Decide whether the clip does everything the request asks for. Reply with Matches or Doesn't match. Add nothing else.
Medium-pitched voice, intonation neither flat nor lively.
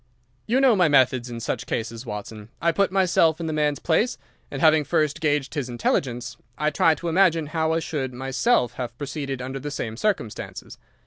Matches